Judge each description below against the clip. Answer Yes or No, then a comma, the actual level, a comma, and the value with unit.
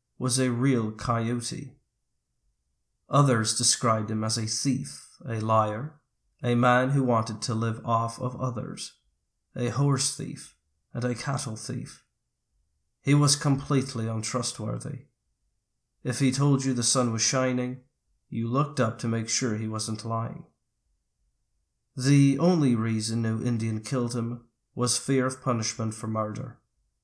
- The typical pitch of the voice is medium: No, low, 120 Hz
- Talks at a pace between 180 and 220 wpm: No, average, 140 wpm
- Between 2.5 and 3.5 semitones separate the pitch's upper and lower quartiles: Yes, average, 2.9 semitones